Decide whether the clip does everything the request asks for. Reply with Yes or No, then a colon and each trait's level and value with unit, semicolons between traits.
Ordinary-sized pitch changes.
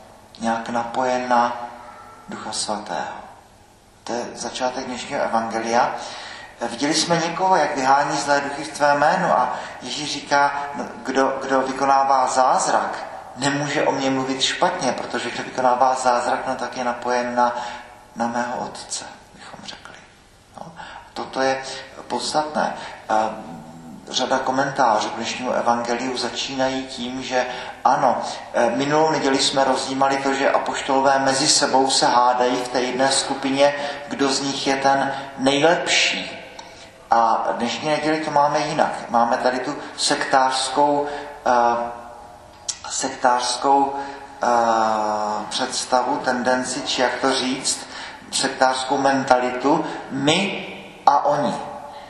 No: narrow, 2.2 semitones